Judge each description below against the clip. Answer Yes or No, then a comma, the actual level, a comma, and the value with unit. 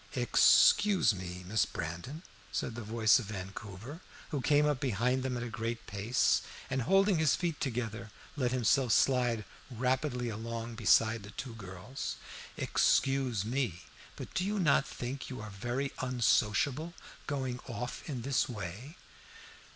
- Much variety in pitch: No, average, 3.8 semitones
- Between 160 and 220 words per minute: No, average, 145 wpm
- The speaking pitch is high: No, low, 125 Hz